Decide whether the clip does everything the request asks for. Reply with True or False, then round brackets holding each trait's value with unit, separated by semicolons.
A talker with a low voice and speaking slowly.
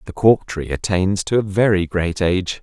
False (95 Hz; 205 wpm)